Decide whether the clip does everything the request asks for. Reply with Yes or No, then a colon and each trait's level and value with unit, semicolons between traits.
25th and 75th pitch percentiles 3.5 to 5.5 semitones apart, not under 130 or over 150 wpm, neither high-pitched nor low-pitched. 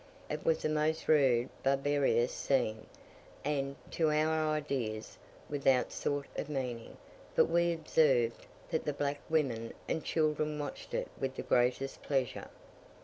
No: average, 3.0 semitones; average, 145 wpm; medium, 145 Hz